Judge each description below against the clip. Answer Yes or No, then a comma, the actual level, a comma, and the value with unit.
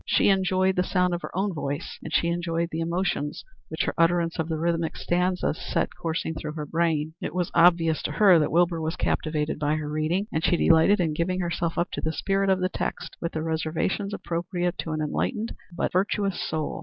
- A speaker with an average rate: No, fast, 215 wpm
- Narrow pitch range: Yes, narrow, 2.3 semitones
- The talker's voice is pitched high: No, medium, 170 Hz